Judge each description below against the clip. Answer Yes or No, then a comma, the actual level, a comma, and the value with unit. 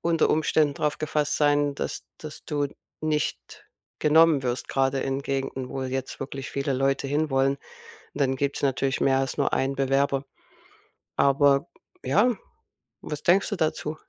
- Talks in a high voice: No, medium, 140 Hz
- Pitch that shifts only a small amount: Yes, narrow, 1.9 semitones